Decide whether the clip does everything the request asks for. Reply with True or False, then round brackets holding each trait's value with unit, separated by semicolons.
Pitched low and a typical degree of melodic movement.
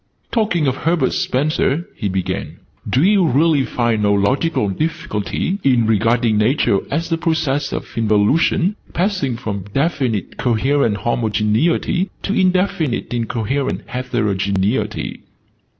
False (130 Hz; 7.1 semitones)